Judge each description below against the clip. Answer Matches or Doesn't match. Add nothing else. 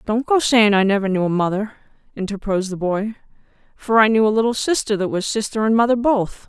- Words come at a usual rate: Doesn't match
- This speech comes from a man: Doesn't match